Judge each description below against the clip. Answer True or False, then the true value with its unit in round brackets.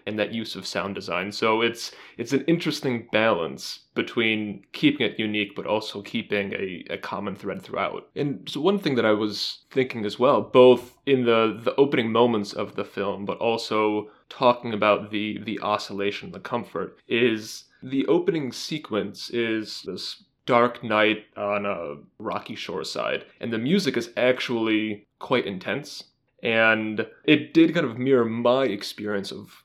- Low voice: True (110 Hz)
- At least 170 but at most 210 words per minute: False (160 wpm)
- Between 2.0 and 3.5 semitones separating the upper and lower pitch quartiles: True (2.8 semitones)